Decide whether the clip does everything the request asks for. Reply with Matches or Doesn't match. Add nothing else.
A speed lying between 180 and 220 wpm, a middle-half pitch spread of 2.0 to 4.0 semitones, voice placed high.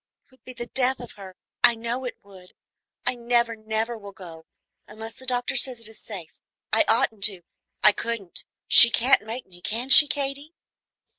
Matches